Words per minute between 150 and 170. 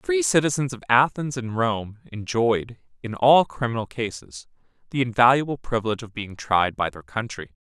Yes: average, 165 wpm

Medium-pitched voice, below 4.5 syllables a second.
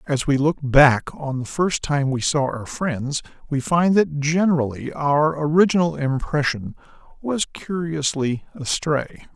Yes: medium, 150 Hz; 4.1 syllables/s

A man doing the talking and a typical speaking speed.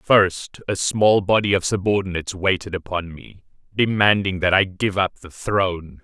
Yes: male; average, 160 wpm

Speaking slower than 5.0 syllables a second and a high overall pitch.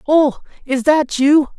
Yes: 3.6 syllables/s; very high, 285 Hz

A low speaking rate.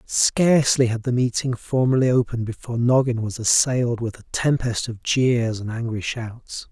No: average, 160 wpm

